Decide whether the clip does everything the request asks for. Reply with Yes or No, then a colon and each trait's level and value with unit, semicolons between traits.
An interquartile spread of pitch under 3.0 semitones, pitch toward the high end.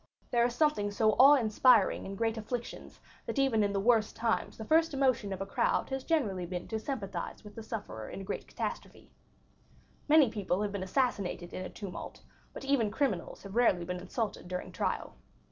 No: average, 4.3 semitones; high, 220 Hz